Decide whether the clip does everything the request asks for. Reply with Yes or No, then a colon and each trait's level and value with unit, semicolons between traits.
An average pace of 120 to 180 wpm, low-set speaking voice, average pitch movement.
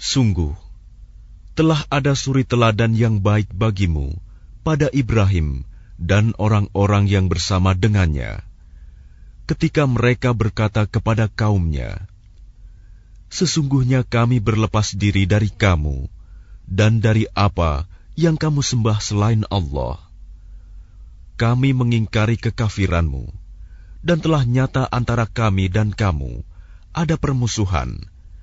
No: average, 95 wpm; low, 105 Hz; average, 4.1 semitones